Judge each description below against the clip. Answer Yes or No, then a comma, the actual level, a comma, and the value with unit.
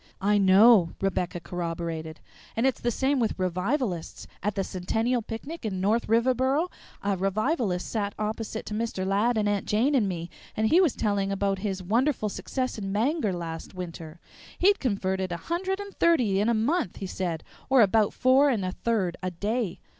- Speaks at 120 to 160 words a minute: No, average, 180 wpm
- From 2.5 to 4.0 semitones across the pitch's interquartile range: No, average, 4.6 semitones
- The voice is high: Yes, high, 210 Hz